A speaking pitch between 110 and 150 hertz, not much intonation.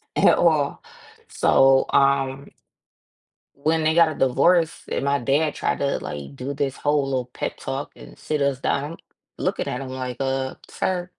Yes: medium, 140 Hz; narrow, 2.3 semitones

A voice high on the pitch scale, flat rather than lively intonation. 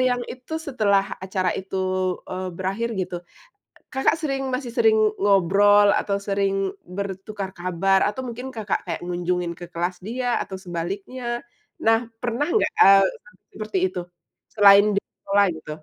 No: high, 200 Hz; average, 3.9 semitones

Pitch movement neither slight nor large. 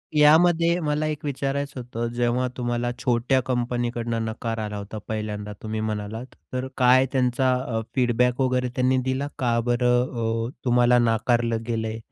No: narrow, 2.3 semitones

